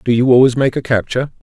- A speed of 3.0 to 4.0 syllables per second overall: No, 6.9 syllables/s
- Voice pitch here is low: Yes, low, 125 Hz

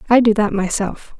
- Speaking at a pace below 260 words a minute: Yes, average, 200 wpm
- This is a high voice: Yes, high, 215 Hz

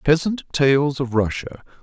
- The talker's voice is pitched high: No, medium, 140 Hz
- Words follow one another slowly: Yes, slow, 130 wpm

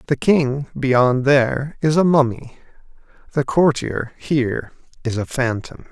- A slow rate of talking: Yes, slow, 130 wpm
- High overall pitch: No, low, 130 Hz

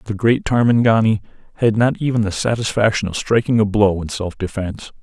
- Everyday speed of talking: Yes, average, 180 wpm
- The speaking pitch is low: Yes, low, 105 Hz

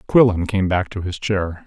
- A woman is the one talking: No, male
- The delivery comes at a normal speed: No, fast, 215 wpm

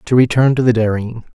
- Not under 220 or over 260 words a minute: Yes, fast, 225 wpm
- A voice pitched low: Yes, low, 120 Hz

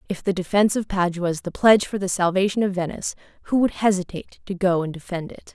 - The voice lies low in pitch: No, high, 190 Hz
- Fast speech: Yes, fast, 225 wpm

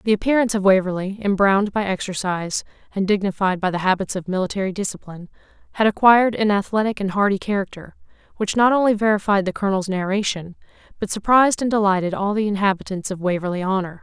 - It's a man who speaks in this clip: No, female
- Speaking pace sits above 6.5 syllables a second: Yes, 6.7 syllables/s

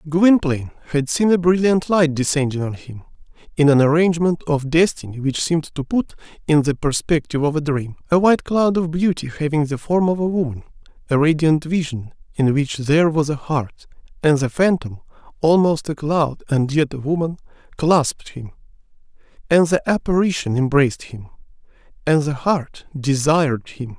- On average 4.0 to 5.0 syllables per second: No, 5.3 syllables/s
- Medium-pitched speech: Yes, medium, 150 Hz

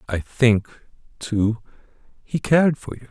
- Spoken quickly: No, slow, 135 wpm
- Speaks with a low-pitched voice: Yes, low, 120 Hz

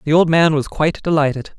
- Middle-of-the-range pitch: Yes, medium, 155 Hz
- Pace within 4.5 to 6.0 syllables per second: No, 6.2 syllables/s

